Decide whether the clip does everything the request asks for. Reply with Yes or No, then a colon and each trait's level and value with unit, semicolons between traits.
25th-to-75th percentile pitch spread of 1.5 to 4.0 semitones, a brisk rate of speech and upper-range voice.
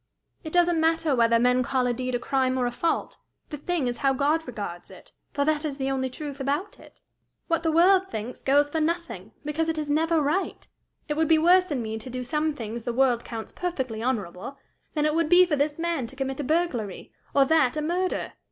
No: average, 4.4 semitones; fast, 225 wpm; very high, 285 Hz